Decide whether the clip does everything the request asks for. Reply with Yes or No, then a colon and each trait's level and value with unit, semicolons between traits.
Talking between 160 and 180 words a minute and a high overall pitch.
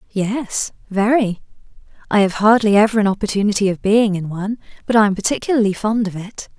Yes: average, 175 wpm; high, 210 Hz